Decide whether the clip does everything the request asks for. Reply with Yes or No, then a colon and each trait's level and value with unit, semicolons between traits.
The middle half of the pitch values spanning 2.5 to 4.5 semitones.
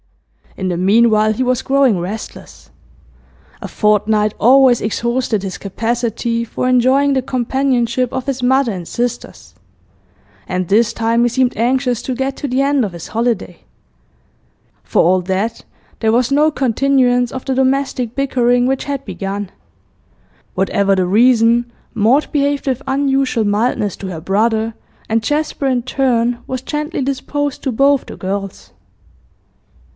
Yes: average, 3.6 semitones